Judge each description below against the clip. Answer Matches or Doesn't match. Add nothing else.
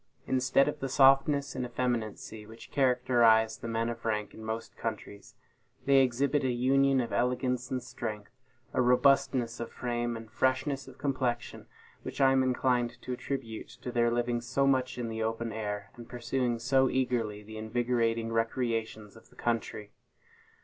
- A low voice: Matches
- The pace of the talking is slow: Doesn't match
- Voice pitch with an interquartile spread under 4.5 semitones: Matches